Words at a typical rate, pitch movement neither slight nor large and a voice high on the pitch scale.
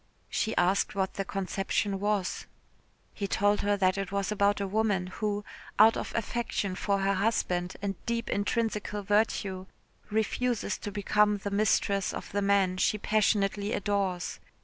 No: average, 150 wpm; narrow, 1.4 semitones; high, 200 Hz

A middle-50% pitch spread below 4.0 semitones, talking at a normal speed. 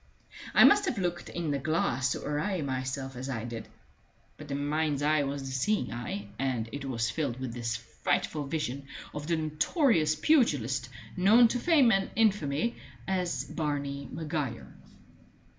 No: average, 4.7 semitones; average, 160 wpm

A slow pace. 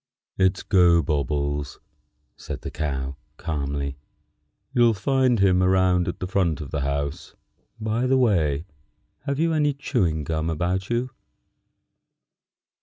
Yes: slow, 120 wpm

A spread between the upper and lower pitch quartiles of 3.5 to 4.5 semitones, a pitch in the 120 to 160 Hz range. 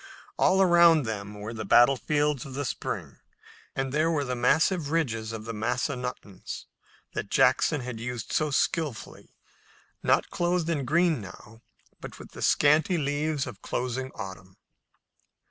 No: wide, 5.5 semitones; low, 135 Hz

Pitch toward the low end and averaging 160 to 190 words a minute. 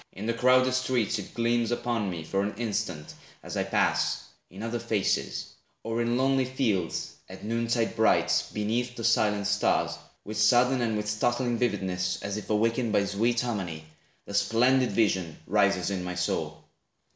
Yes: low, 110 Hz; average, 170 wpm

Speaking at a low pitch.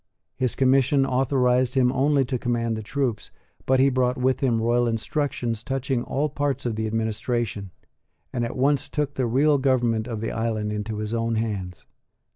Yes: low, 125 Hz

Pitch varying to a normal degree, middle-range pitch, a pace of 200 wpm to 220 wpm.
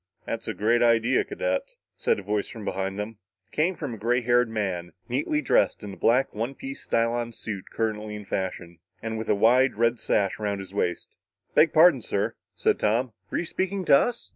No: average, 4.2 semitones; low, 115 Hz; fast, 205 wpm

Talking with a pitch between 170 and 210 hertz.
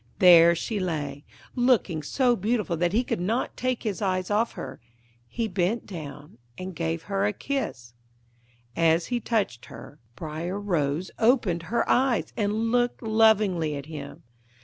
Yes: high, 190 Hz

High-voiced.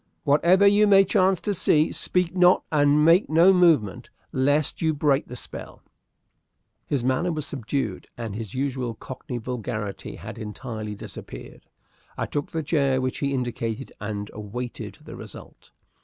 No: medium, 140 Hz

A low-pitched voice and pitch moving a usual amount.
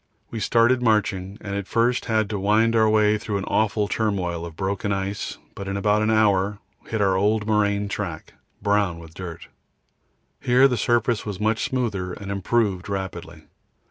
No: low, 105 Hz; narrow, 2.2 semitones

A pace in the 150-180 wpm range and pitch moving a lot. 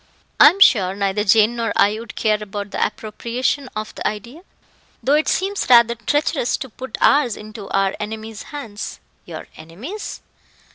No: average, 160 wpm; average, 4.1 semitones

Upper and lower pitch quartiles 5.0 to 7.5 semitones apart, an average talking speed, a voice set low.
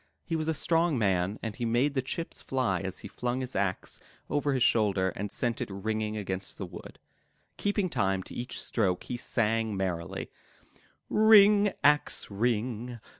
Yes: wide, 5.6 semitones; average, 170 wpm; low, 115 Hz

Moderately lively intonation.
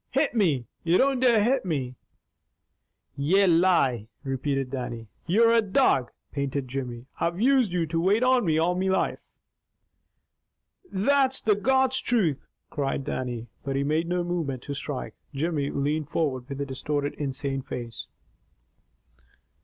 No: wide, 6.7 semitones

